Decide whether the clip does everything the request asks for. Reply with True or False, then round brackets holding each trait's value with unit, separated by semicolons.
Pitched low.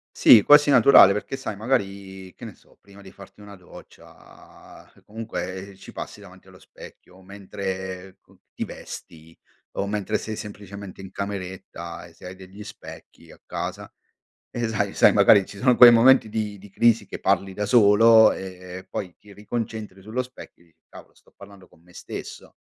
True (100 Hz)